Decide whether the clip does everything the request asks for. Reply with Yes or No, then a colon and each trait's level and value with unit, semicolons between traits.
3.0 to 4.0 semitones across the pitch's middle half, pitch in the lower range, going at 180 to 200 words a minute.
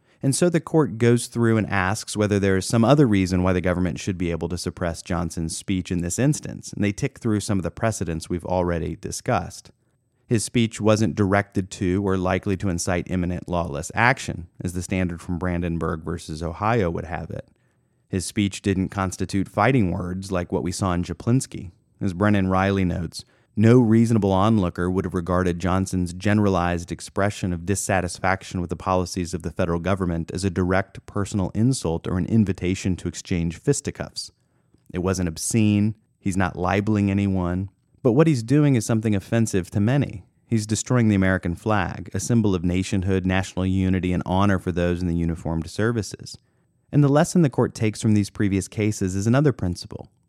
Yes: average, 3.5 semitones; very low, 95 Hz; average, 185 wpm